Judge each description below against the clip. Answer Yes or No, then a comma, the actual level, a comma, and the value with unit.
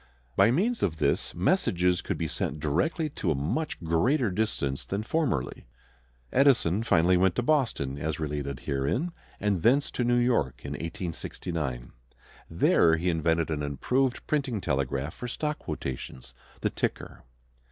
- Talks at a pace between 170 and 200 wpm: No, average, 145 wpm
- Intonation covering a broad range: Yes, wide, 8.7 semitones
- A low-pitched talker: Yes, very low, 90 Hz